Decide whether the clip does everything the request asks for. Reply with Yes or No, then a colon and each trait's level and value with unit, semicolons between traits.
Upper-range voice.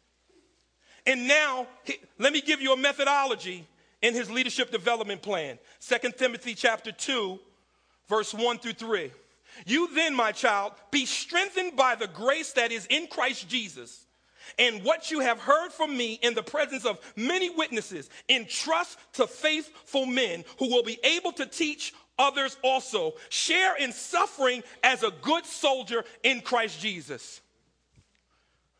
Yes: very high, 255 Hz